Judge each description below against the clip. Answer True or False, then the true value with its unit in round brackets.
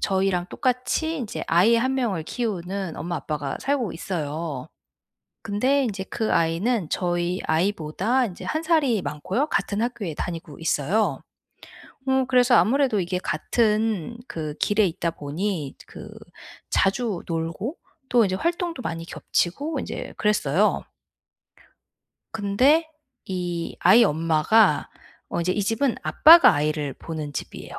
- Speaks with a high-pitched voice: True (195 Hz)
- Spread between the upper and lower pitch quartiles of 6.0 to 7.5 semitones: True (6.5 semitones)